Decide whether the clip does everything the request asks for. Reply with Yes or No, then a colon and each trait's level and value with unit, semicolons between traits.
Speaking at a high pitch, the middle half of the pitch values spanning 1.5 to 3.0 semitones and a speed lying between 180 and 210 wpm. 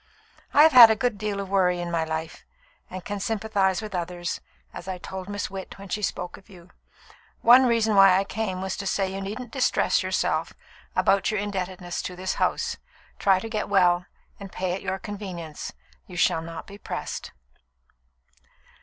Yes: high, 195 Hz; narrow, 2.4 semitones; average, 190 wpm